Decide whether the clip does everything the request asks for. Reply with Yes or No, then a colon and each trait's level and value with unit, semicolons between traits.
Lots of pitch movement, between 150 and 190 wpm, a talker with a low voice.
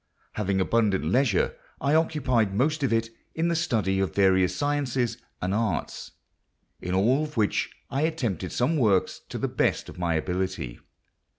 Yes: wide, 6.5 semitones; average, 160 wpm; low, 115 Hz